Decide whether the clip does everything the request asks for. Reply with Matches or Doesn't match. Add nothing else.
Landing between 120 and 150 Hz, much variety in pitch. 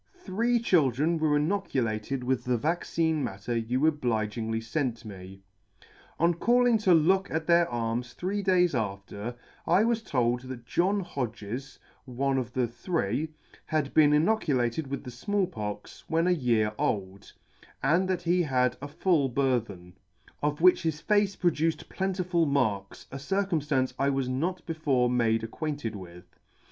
Matches